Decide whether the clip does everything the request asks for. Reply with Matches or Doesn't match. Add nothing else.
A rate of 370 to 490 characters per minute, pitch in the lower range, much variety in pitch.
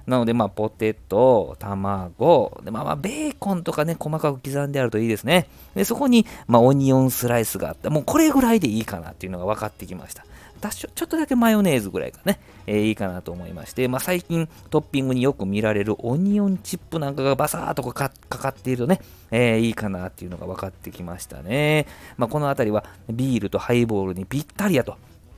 Matches